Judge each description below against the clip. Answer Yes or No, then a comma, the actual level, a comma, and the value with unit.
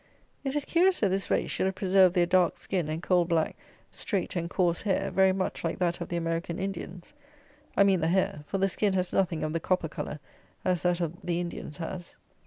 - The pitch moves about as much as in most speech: No, narrow, 2.1 semitones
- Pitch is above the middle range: No, medium, 180 Hz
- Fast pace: Yes, fast, 220 wpm